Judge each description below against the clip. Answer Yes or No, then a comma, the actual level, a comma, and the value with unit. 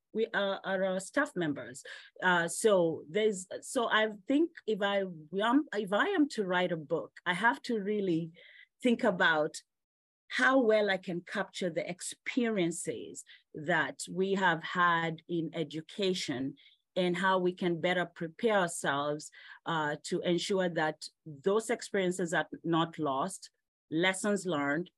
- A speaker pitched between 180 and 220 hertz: Yes, medium, 185 Hz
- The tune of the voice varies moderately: Yes, average, 3.9 semitones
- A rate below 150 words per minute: Yes, average, 140 wpm